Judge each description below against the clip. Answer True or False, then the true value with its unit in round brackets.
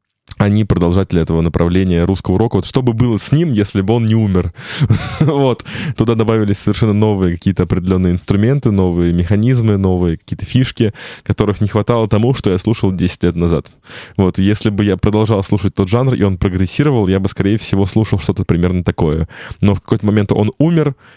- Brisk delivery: True (185 wpm)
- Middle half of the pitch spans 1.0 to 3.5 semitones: True (3.1 semitones)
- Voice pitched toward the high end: False (105 Hz)